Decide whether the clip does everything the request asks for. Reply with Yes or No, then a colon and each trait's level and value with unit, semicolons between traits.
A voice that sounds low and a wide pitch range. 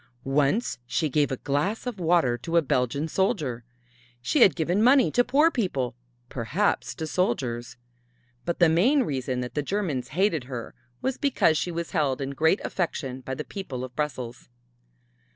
No: medium, 150 Hz; wide, 6.7 semitones